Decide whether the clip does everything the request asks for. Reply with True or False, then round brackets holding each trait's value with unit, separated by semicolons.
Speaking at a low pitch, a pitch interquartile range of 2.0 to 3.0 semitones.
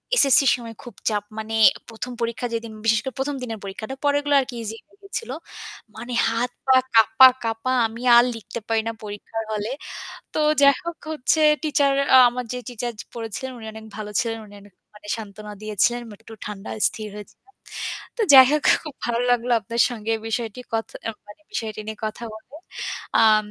False (230 Hz; 2.6 semitones)